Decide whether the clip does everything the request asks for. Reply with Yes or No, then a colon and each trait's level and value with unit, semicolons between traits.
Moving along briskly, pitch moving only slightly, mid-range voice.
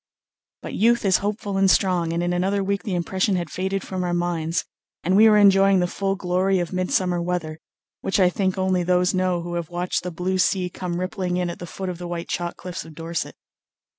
Yes: fast, 225 wpm; narrow, 1.7 semitones; medium, 180 Hz